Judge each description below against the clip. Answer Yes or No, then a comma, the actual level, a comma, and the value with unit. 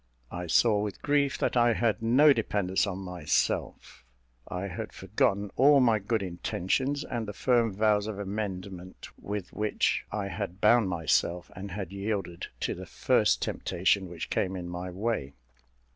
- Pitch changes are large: No, average, 3.6 semitones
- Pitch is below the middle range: Yes, low, 100 Hz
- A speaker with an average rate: Yes, average, 160 wpm